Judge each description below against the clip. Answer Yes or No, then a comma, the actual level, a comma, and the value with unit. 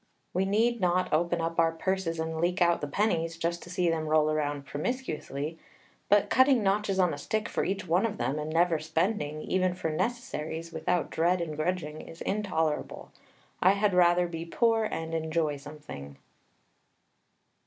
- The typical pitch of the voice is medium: Yes, medium, 170 Hz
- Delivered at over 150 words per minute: Yes, average, 170 wpm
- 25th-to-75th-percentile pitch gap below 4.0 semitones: Yes, average, 3.4 semitones